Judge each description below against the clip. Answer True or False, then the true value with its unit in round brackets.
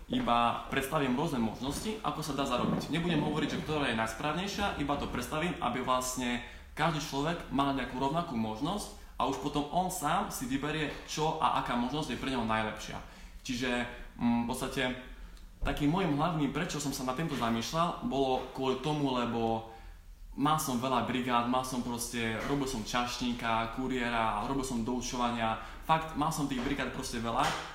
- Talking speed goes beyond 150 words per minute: True (165 wpm)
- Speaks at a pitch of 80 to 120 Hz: False (130 Hz)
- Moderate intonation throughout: True (3.7 semitones)